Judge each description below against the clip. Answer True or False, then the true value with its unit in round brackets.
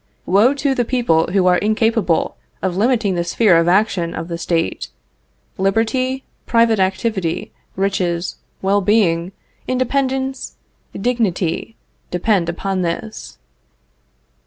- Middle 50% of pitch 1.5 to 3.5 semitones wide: False (4.9 semitones)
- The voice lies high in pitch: True (195 Hz)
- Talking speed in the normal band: False (110 wpm)